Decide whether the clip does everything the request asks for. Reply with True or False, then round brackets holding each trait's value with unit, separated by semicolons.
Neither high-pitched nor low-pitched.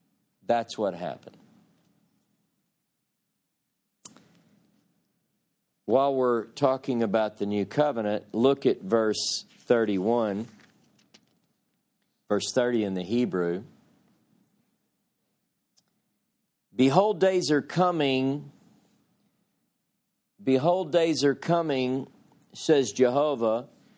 False (130 Hz)